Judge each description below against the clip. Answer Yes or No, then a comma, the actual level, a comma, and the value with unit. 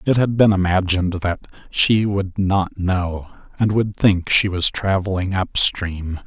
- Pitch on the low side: Yes, very low, 95 Hz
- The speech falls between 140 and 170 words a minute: Yes, average, 155 wpm